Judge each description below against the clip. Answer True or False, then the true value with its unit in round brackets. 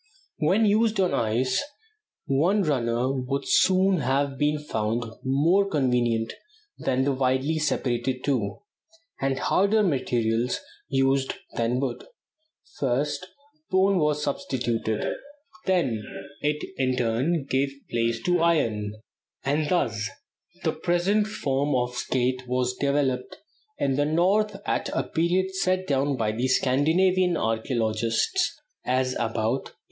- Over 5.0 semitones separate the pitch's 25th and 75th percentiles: True (5.5 semitones)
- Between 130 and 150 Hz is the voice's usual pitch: True (135 Hz)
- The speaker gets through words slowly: True (120 wpm)